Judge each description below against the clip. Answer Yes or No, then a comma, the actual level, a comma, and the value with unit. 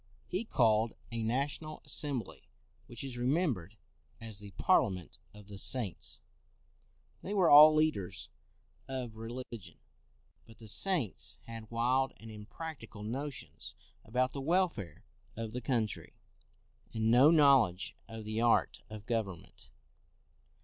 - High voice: No, low, 115 Hz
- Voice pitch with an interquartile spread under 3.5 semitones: No, average, 4.2 semitones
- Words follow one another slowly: Yes, slow, 130 wpm